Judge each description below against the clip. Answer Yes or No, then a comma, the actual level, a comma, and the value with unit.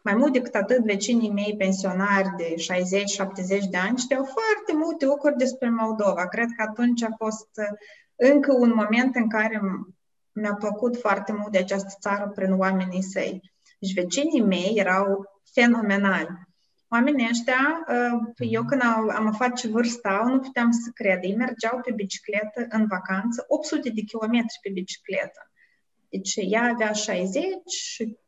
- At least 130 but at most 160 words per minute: Yes, average, 150 wpm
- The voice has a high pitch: Yes, high, 220 Hz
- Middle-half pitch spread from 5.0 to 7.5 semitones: No, average, 3.9 semitones